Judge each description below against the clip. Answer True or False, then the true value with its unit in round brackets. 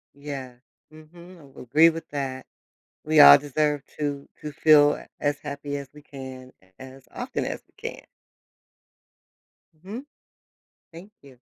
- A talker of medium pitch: True (145 Hz)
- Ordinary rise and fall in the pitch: False (2.2 semitones)